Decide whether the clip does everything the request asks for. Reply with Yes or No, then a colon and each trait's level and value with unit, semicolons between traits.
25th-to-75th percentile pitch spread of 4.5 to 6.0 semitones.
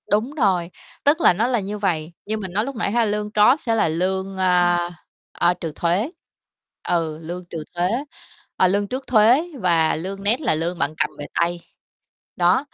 No: average, 4.0 semitones